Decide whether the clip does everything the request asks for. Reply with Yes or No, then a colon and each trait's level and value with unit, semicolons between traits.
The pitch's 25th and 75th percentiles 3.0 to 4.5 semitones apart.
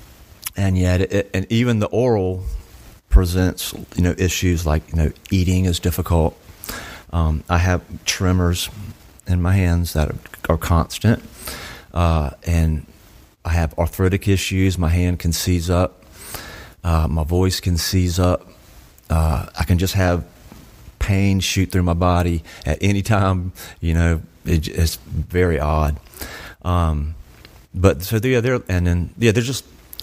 No: narrow, 2.6 semitones